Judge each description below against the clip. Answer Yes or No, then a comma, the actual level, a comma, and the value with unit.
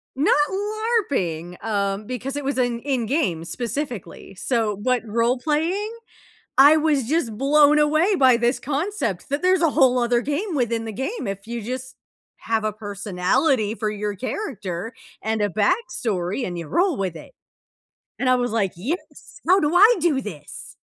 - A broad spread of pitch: Yes, wide, 6.1 semitones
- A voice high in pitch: Yes, high, 245 Hz